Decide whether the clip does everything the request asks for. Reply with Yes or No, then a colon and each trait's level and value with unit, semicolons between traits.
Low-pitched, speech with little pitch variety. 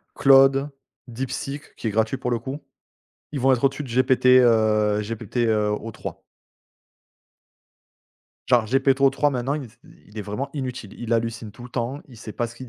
No: low, 120 Hz; average, 3.2 semitones